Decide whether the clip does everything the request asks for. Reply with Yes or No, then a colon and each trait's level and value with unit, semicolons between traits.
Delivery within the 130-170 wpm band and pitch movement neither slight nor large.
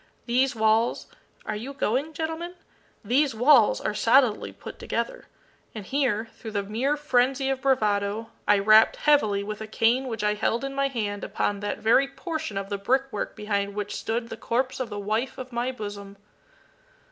No: average, 180 wpm; average, 4.3 semitones